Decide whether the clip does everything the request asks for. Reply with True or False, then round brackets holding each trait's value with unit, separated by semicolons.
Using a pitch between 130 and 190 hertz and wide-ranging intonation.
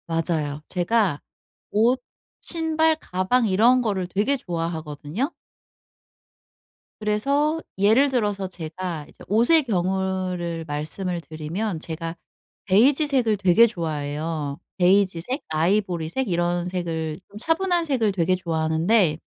True (185 Hz; 5.7 semitones)